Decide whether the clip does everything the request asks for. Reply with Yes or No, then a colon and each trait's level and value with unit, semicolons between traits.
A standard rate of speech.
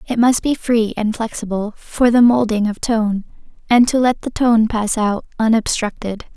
Yes: average, 180 wpm